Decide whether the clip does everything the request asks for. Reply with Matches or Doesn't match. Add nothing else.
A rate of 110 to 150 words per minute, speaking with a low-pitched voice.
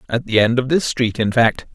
Doesn't match